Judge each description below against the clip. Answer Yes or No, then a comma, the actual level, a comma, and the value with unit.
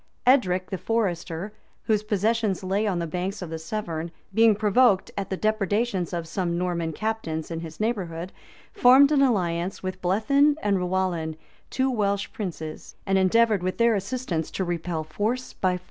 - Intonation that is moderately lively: Yes, average, 4.1 semitones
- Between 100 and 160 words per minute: No, average, 170 wpm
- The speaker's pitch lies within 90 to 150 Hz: No, high, 190 Hz